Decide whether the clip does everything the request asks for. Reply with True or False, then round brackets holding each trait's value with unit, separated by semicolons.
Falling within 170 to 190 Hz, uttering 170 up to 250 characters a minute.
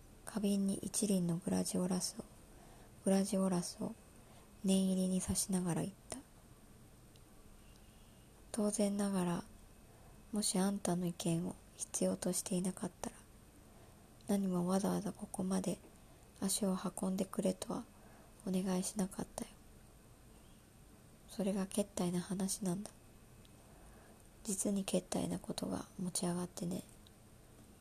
True (185 Hz; 235 characters per minute)